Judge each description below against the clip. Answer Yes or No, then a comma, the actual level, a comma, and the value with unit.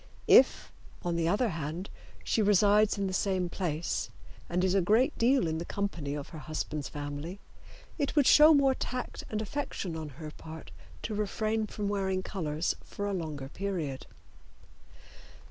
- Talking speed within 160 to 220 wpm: Yes, average, 165 wpm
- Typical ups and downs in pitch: Yes, average, 4.9 semitones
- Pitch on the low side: No, medium, 185 Hz